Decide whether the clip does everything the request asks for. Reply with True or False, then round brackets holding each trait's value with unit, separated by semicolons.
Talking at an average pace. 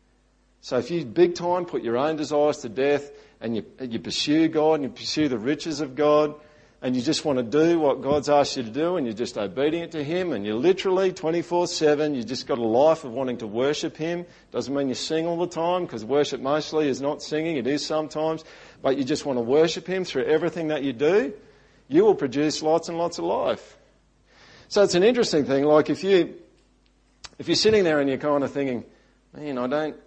False (225 wpm)